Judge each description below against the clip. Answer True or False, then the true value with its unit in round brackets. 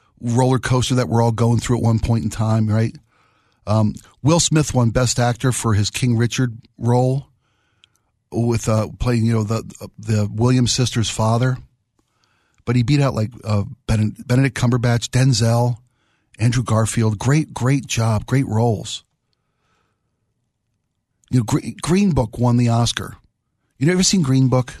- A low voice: True (120 Hz)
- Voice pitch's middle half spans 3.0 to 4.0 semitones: False (2.4 semitones)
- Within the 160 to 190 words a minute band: False (150 wpm)